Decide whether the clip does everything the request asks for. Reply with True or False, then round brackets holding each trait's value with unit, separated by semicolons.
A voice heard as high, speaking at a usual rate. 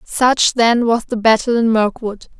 True (225 Hz; 175 wpm)